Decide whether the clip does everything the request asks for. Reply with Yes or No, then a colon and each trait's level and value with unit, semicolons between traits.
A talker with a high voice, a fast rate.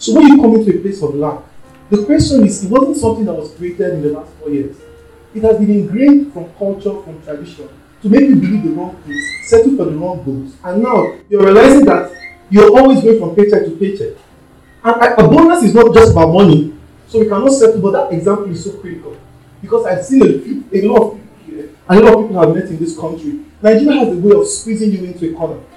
Yes: high, 205 Hz; fast, 240 wpm